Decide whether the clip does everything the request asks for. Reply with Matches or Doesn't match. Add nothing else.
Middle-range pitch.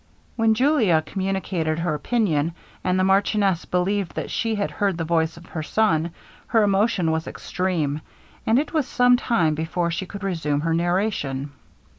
Matches